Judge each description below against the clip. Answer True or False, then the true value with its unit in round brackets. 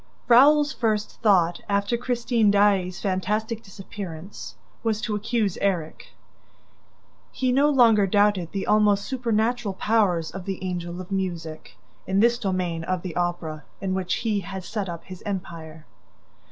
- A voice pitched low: False (195 Hz)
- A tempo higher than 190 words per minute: False (140 wpm)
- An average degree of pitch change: True (3.5 semitones)